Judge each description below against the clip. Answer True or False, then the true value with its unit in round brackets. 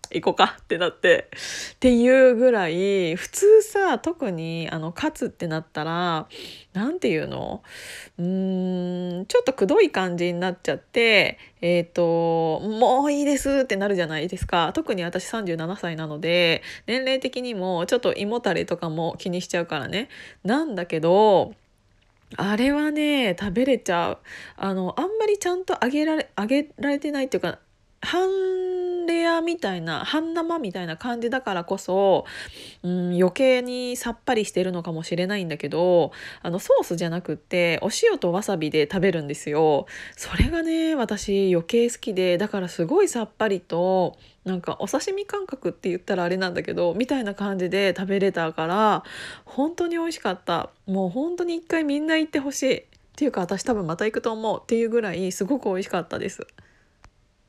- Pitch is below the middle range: False (200 Hz)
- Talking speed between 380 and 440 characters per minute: False (340 characters per minute)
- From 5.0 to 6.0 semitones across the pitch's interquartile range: False (7.5 semitones)